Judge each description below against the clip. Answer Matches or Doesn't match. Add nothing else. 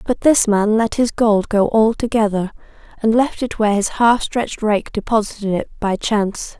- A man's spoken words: Doesn't match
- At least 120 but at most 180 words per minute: Doesn't match